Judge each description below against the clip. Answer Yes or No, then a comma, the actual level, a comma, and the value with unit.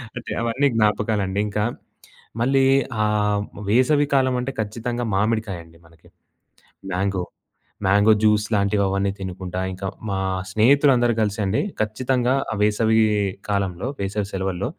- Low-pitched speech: Yes, low, 105 Hz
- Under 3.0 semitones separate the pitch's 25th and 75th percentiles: No, average, 3.3 semitones